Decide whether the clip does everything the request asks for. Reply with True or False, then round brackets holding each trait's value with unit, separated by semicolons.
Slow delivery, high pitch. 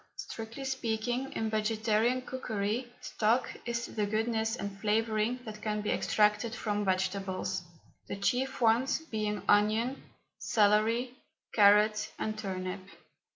True (115 wpm; 215 Hz)